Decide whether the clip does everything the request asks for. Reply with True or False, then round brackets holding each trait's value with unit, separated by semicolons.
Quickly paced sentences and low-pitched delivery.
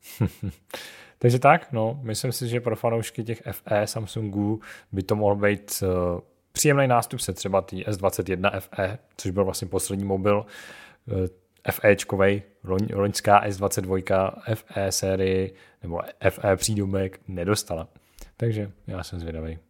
False (130 wpm; 100 Hz)